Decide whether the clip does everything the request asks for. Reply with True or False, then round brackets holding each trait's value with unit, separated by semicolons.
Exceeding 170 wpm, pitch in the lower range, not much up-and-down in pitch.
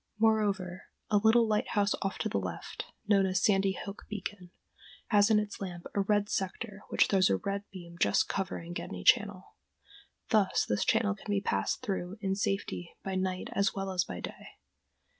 False (180 wpm; 195 Hz; 2.0 semitones)